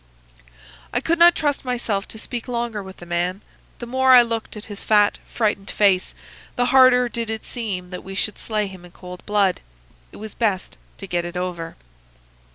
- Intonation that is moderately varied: Yes, average, 4.3 semitones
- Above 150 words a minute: Yes, average, 190 wpm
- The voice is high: Yes, high, 210 Hz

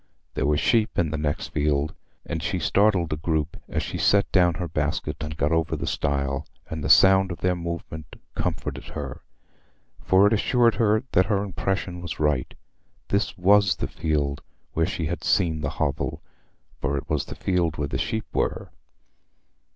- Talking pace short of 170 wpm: No, average, 175 wpm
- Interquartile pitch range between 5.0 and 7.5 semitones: No, average, 4.2 semitones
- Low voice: Yes, very low, 85 Hz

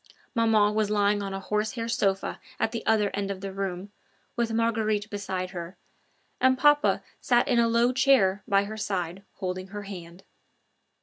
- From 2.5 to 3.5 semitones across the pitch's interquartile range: Yes, average, 3.0 semitones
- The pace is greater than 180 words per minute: No, average, 170 wpm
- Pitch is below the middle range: No, high, 205 Hz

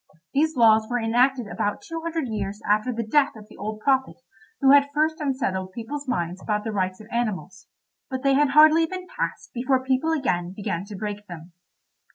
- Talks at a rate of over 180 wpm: Yes, average, 195 wpm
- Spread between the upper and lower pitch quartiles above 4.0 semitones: Yes, average, 5.3 semitones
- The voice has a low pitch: No, high, 235 Hz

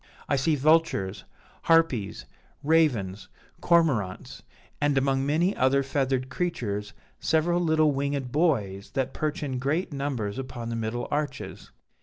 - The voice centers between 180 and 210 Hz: No, medium, 140 Hz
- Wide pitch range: No, average, 4.5 semitones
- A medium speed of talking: No, slow, 125 wpm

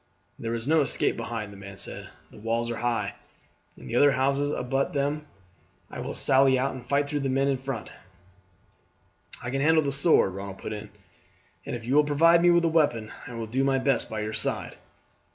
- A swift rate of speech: Yes, fast, 210 wpm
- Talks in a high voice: No, low, 135 Hz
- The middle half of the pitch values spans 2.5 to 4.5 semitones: Yes, average, 3.7 semitones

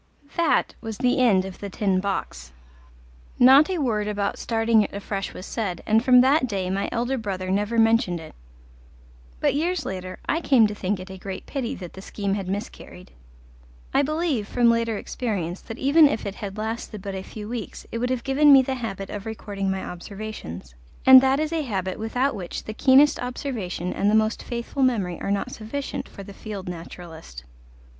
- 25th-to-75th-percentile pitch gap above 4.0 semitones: Yes, average, 4.7 semitones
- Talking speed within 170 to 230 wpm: Yes, average, 195 wpm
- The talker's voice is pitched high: Yes, high, 215 Hz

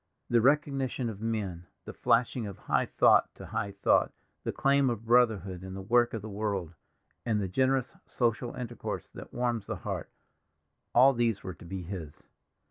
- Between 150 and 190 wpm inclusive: Yes, average, 170 wpm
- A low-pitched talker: Yes, low, 115 Hz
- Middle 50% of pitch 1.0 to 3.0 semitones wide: No, average, 4.0 semitones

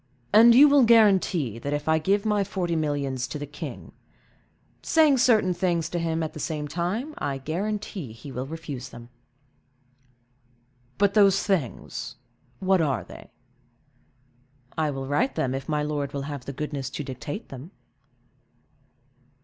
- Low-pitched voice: No, medium, 160 Hz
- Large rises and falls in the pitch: Yes, wide, 6.0 semitones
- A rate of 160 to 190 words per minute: No, average, 150 wpm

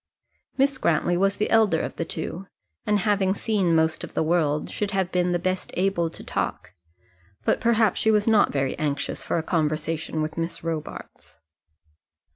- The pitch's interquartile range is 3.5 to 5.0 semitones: Yes, average, 4.2 semitones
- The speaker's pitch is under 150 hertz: No, medium, 175 Hz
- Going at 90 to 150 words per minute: No, average, 175 wpm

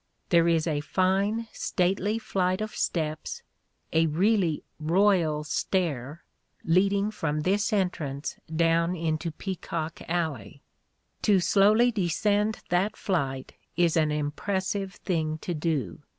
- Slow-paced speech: Yes, slow, 120 wpm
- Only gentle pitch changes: No, average, 4.0 semitones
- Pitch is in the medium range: Yes, medium, 170 Hz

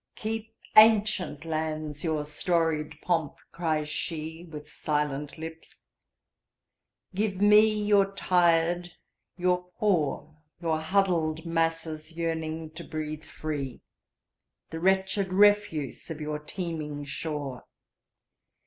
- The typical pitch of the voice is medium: Yes, medium, 165 Hz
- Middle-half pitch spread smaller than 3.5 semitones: Yes, average, 3.0 semitones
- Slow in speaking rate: Yes, slow, 90 wpm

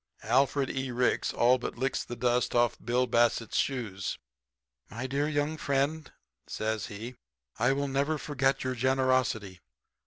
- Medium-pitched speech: No, low, 130 Hz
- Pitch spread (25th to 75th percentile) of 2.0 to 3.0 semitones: Yes, narrow, 2.4 semitones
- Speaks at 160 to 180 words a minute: No, average, 150 wpm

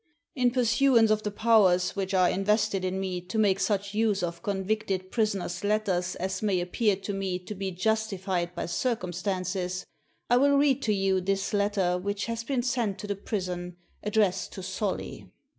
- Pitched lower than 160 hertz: No, high, 200 Hz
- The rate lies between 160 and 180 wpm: Yes, average, 175 wpm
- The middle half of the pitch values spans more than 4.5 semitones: No, average, 2.9 semitones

